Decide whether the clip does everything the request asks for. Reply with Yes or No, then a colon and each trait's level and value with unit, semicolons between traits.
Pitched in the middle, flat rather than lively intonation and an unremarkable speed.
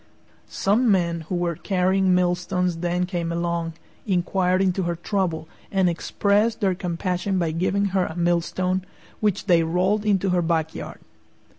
Yes: medium, 180 Hz; narrow, 2.1 semitones; average, 150 wpm